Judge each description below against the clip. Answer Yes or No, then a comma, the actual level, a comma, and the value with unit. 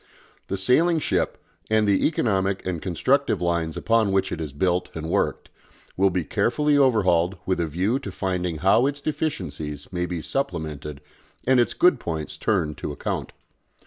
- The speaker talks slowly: No, average, 165 wpm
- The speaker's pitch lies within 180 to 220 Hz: No, very low, 95 Hz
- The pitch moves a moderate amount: No, wide, 6.3 semitones